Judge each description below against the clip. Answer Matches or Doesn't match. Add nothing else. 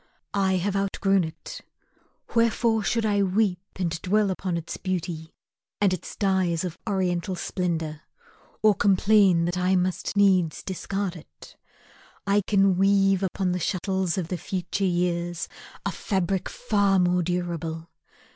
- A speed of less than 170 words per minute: Matches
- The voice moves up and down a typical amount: Doesn't match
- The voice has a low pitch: Doesn't match